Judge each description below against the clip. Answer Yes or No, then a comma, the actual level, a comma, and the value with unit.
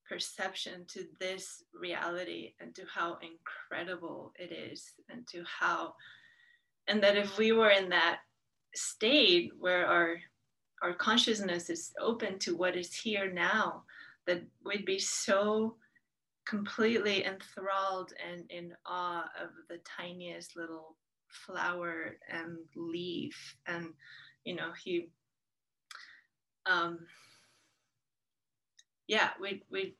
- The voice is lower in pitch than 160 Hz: No, medium, 185 Hz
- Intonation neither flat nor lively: Yes, average, 3.3 semitones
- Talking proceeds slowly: Yes, slow, 110 wpm